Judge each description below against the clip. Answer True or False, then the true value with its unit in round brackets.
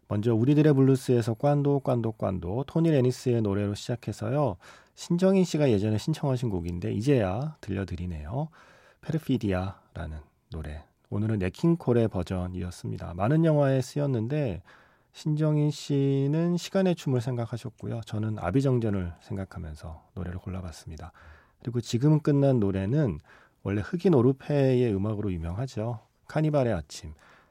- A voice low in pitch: True (120 Hz)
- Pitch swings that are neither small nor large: False (6.8 semitones)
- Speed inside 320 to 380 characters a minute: True (340 characters per minute)